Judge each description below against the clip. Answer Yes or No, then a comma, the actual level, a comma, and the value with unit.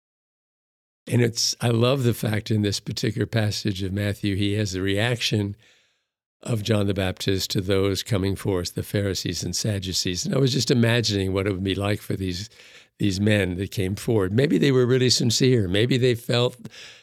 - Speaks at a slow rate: No, average, 185 wpm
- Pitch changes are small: No, average, 3.3 semitones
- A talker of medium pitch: No, low, 105 Hz